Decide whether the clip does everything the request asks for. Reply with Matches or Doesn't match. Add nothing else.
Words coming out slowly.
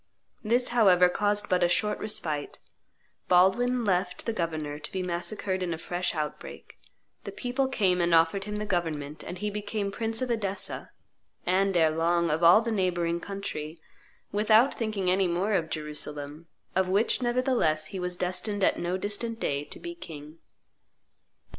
Doesn't match